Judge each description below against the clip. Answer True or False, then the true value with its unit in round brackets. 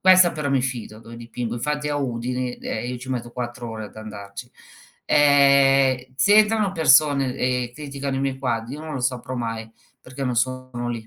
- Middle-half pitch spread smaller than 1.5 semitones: False (2.7 semitones)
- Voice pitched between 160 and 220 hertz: False (130 Hz)